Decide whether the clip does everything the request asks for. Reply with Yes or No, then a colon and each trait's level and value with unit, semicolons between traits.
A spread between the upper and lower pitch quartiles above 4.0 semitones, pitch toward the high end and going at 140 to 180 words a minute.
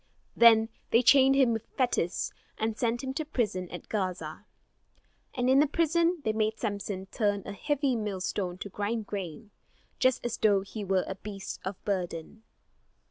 Yes: average, 4.5 semitones; high, 215 Hz; average, 165 wpm